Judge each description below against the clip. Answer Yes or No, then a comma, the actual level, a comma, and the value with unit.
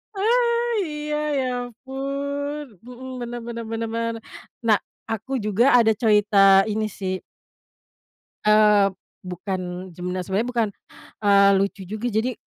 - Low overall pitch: No, high, 225 Hz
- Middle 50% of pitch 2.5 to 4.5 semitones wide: No, average, 4.9 semitones